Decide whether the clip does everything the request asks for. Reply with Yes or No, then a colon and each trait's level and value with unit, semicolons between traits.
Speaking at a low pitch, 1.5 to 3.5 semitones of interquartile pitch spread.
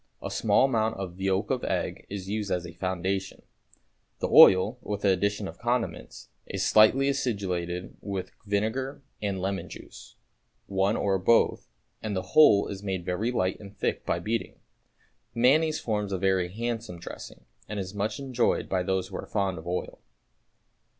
Yes: low, 100 Hz; average, 3.1 semitones